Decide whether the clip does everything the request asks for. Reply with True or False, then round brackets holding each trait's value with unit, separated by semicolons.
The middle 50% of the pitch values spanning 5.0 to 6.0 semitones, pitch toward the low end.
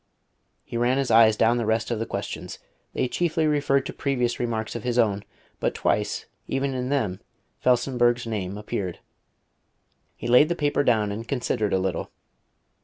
False (3.4 semitones; 120 Hz)